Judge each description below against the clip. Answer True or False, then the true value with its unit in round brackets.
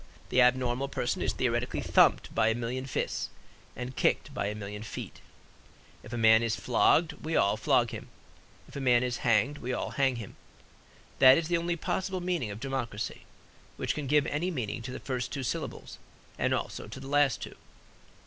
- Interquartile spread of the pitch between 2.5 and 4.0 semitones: True (3.2 semitones)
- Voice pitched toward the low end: True (125 Hz)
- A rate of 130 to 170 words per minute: False (190 wpm)